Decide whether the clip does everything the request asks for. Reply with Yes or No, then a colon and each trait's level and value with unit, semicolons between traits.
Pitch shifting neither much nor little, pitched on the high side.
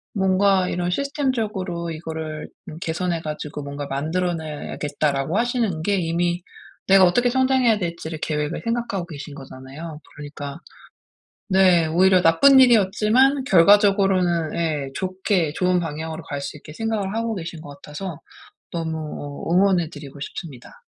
No: average, 4.1 semitones; medium, 170 Hz